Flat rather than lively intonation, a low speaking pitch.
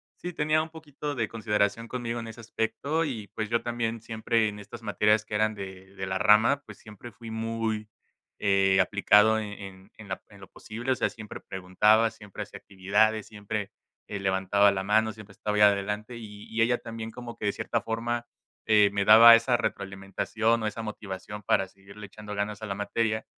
Yes: narrow, 2.1 semitones; low, 110 Hz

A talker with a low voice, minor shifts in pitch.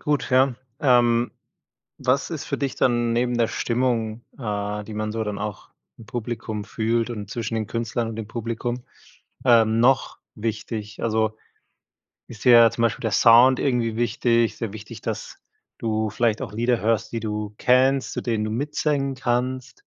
Yes: low, 115 Hz; narrow, 2.1 semitones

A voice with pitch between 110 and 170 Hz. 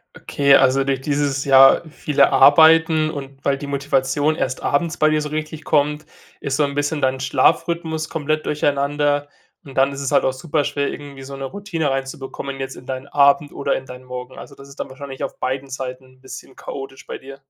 Yes: medium, 140 Hz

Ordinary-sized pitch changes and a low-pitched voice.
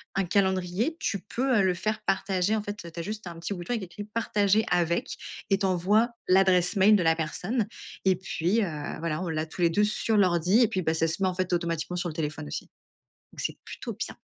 No: average, 3.4 semitones; medium, 185 Hz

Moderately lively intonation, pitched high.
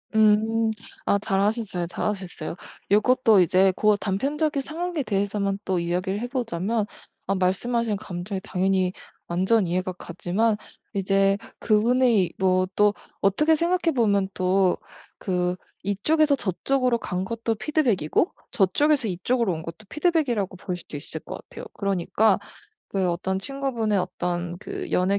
Yes: average, 4.3 semitones; high, 200 Hz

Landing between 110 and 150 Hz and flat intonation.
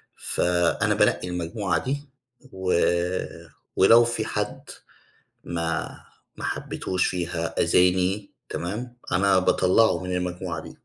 No: very low, 90 Hz; narrow, 2.3 semitones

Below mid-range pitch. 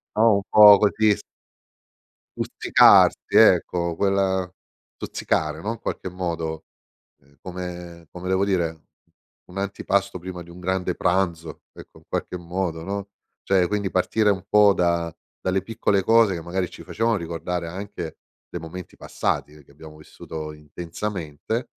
Yes: very low, 90 Hz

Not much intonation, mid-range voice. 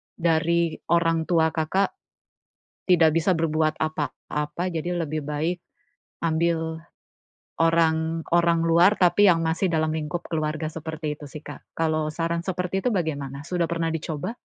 Yes: narrow, 1.5 semitones; medium, 165 Hz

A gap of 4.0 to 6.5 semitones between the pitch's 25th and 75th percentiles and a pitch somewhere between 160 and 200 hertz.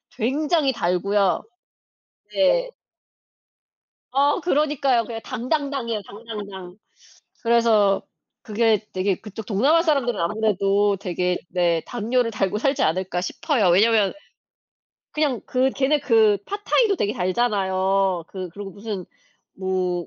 No: average, 5.3 semitones; high, 215 Hz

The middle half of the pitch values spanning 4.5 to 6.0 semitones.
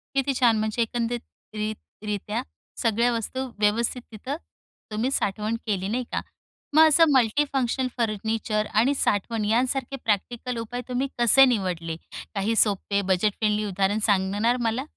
No: average, 2.9 semitones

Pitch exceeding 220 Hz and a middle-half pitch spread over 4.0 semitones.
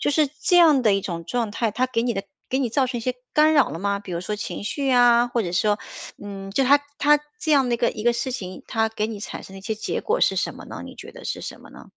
Yes: high, 235 Hz; average, 4.6 semitones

